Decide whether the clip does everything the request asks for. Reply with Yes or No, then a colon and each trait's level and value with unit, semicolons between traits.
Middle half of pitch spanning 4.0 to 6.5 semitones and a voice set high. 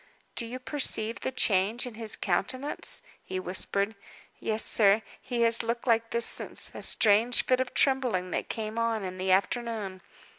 No: average, 3.3 semitones; high, 225 Hz